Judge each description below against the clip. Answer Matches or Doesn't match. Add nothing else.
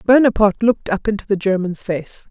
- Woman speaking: Matches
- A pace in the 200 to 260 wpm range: Doesn't match